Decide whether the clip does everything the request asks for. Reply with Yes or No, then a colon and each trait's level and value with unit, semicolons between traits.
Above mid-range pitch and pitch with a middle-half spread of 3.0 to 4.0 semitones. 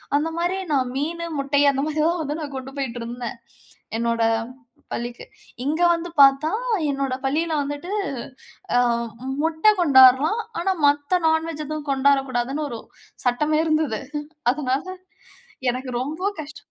Yes: very high, 285 Hz; average, 3.3 semitones